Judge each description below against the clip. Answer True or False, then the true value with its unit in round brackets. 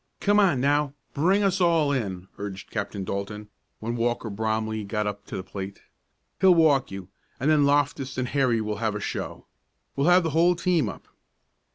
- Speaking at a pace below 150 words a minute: False (185 wpm)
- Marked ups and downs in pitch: True (6.9 semitones)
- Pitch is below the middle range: True (125 Hz)